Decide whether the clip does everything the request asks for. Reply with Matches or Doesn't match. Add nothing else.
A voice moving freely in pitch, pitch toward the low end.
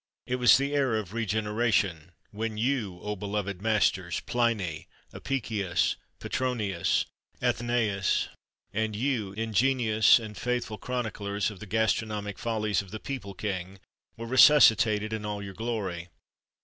Doesn't match